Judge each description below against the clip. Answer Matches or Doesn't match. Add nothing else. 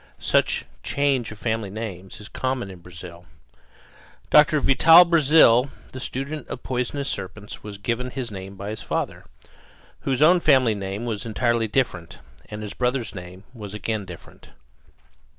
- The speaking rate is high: Doesn't match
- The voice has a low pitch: Matches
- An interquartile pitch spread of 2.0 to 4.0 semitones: Doesn't match